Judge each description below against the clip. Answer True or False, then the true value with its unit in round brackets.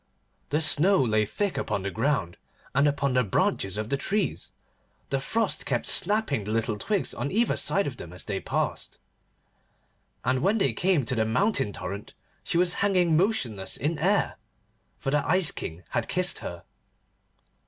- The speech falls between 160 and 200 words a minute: True (170 wpm)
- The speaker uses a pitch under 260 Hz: True (140 Hz)